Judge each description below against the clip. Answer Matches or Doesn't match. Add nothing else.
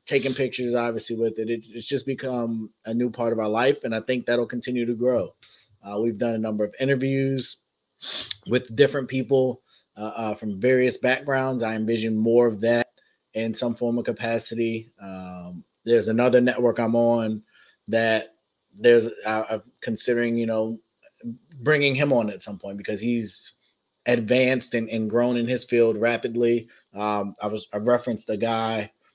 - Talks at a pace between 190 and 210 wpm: Doesn't match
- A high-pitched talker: Doesn't match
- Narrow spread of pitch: Matches